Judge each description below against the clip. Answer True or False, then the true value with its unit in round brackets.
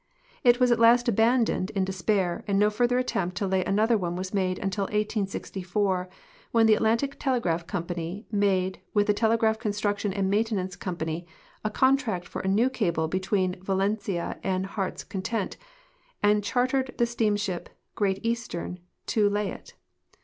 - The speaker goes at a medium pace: True (160 wpm)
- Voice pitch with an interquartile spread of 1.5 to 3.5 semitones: True (3.2 semitones)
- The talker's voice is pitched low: False (205 Hz)